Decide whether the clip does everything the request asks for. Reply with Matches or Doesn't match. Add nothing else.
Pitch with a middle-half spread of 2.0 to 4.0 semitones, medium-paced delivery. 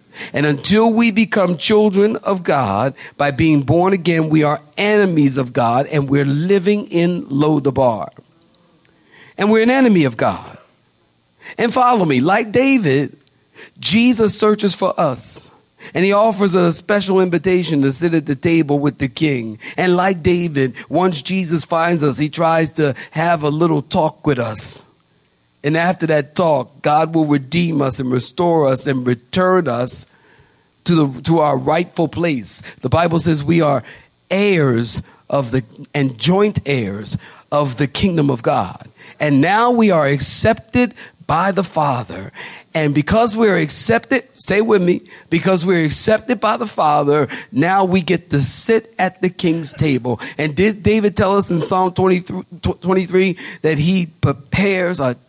Doesn't match